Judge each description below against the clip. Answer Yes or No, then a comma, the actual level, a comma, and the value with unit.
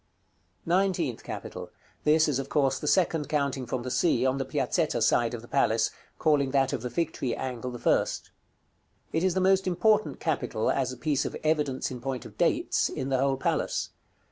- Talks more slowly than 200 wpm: No, fast, 205 wpm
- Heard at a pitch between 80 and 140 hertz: Yes, low, 135 Hz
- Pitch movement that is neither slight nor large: Yes, average, 4.0 semitones